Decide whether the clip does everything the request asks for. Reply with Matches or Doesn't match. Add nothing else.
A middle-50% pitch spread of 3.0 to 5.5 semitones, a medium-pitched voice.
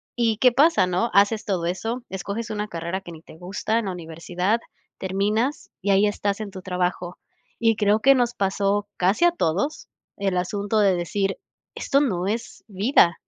Doesn't match